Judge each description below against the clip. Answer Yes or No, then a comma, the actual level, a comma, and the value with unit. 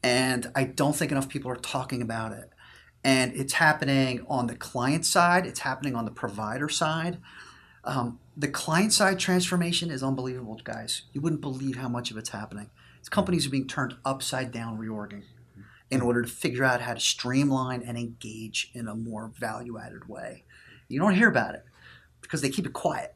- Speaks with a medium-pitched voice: No, low, 130 Hz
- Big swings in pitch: No, average, 3.3 semitones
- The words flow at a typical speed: Yes, average, 190 wpm